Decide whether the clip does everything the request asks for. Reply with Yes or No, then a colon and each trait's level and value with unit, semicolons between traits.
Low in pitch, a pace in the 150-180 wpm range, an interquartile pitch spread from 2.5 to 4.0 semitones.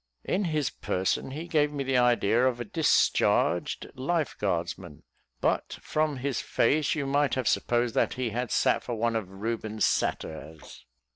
No: low, 125 Hz; average, 160 wpm; average, 4.8 semitones